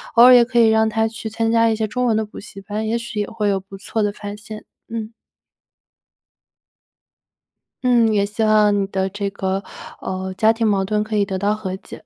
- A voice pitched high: Yes, high, 215 Hz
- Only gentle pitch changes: Yes, narrow, 1.8 semitones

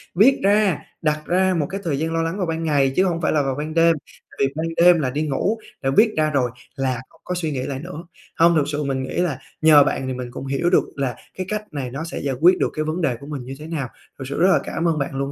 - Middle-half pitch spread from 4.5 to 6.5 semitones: No, average, 3.8 semitones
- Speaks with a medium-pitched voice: Yes, medium, 155 Hz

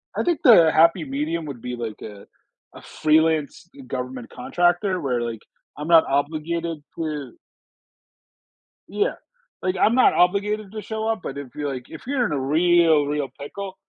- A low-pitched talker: No, medium, 160 Hz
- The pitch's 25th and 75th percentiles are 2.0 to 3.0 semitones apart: No, average, 4.6 semitones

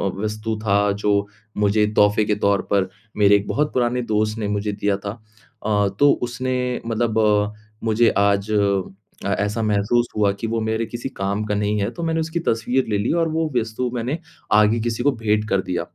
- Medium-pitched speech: No, low, 110 Hz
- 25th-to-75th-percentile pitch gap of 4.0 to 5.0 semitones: No, narrow, 2.6 semitones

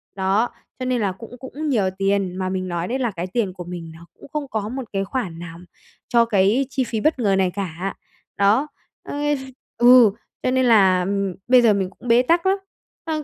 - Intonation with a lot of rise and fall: No, average, 5.0 semitones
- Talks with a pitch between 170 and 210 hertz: Yes, high, 205 Hz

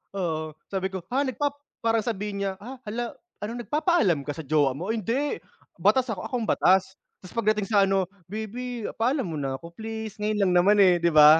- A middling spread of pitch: Yes, average, 4.6 semitones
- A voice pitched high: Yes, high, 210 Hz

